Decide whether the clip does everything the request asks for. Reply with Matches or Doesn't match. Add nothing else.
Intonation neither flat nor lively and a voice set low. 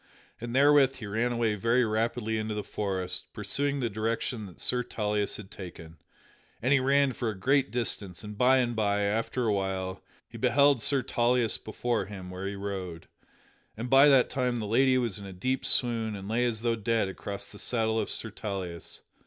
Matches